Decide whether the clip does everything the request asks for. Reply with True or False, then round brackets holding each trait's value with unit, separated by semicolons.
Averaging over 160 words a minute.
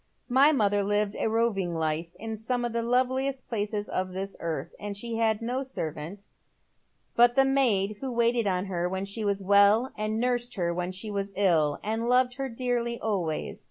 True (185 wpm)